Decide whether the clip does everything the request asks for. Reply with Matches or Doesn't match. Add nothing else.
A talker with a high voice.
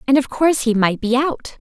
Matches